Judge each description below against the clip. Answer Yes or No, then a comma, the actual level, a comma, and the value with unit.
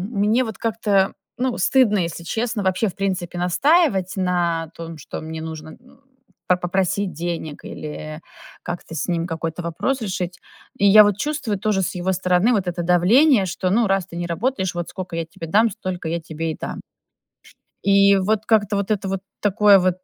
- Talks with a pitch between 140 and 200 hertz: Yes, medium, 185 Hz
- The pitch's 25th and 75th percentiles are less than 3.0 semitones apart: No, average, 3.6 semitones